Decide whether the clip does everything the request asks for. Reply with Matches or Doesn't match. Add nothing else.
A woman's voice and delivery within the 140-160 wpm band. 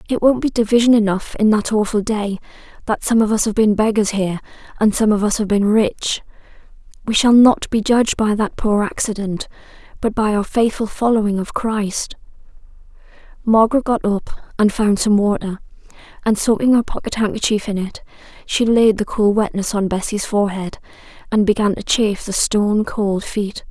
Doesn't match